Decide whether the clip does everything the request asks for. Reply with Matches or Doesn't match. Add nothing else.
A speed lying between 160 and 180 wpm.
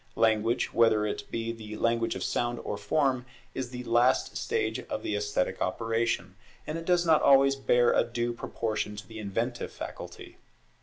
Matches